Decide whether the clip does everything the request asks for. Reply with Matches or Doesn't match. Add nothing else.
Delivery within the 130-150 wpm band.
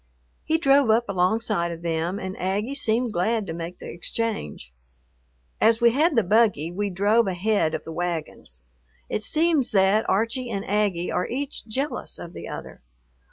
Doesn't match